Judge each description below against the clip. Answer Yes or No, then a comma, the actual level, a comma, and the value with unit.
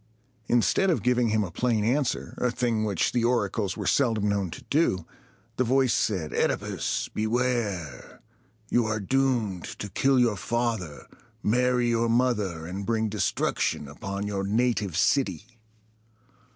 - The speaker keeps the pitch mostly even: No, average, 3.8 semitones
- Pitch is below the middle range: Yes, low, 110 Hz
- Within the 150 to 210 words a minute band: No, average, 140 wpm